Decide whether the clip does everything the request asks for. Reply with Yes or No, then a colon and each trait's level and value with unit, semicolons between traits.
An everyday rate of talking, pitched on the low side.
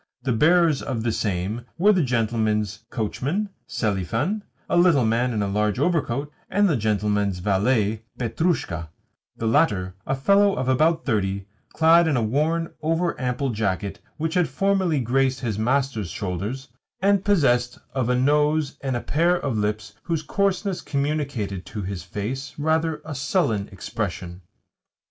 Yes: average, 150 wpm; low, 130 Hz